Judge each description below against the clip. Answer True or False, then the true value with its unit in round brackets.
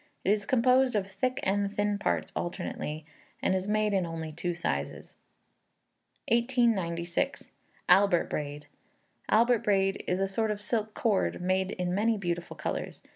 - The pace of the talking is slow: False (145 wpm)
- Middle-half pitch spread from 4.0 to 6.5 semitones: False (3.5 semitones)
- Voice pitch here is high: True (195 Hz)